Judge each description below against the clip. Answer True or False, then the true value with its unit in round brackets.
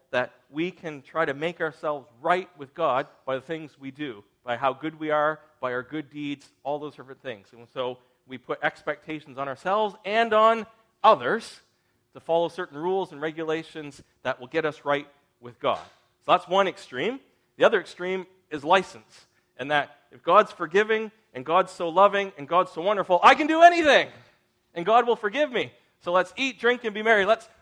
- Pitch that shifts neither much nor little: False (5.7 semitones)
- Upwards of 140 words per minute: True (195 wpm)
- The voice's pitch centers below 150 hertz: False (160 Hz)